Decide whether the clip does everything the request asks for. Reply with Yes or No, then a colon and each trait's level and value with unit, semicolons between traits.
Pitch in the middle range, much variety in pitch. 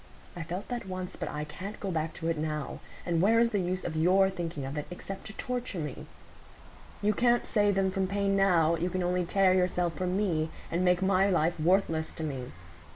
No: medium, 180 Hz; average, 3.0 semitones